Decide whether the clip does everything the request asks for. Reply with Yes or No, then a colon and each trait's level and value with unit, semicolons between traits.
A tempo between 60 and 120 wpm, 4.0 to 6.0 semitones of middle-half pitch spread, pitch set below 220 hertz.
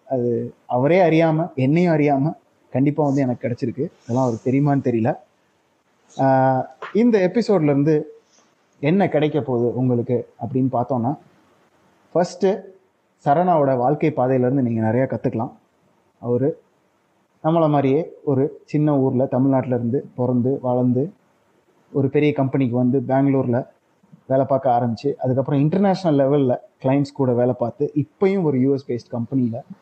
No: average, 115 wpm; average, 3.2 semitones; low, 135 Hz